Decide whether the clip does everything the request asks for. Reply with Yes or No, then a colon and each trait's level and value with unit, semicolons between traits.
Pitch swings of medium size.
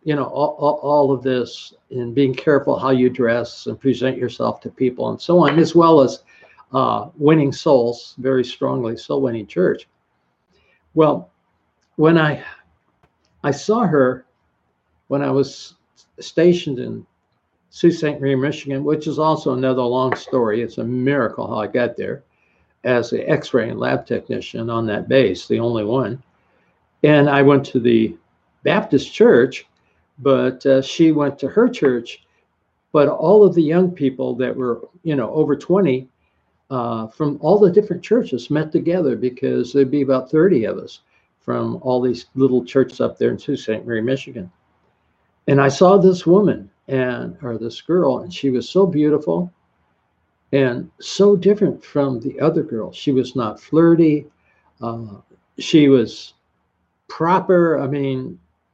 Yes: average, 4.0 semitones